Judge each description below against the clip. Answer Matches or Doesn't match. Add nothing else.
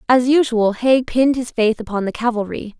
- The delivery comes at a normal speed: Matches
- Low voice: Doesn't match